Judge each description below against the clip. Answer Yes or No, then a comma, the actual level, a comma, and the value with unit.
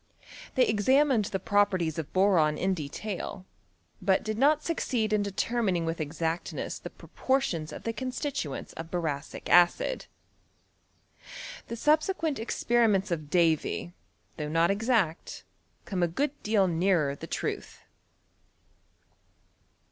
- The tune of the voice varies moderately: No, wide, 6.0 semitones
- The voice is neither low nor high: No, high, 195 Hz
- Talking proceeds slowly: Yes, slow, 120 wpm